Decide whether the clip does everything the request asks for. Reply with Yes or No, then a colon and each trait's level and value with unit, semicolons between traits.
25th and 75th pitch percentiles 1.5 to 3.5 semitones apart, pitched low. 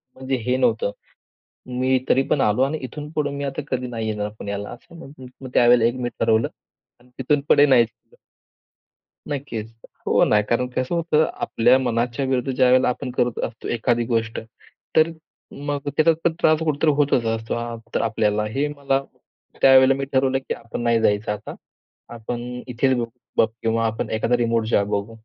Yes: average, 2.9 semitones; low, 125 Hz